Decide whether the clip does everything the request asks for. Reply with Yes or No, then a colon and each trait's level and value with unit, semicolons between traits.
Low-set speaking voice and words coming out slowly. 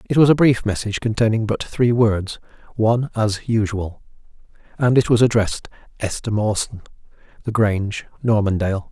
Yes: low, 110 Hz; slow, 130 wpm